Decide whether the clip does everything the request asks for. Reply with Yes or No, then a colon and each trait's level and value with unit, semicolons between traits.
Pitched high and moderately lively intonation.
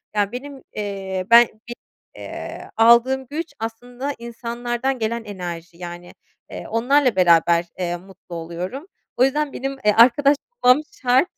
No: high, 235 Hz; wide, 5.7 semitones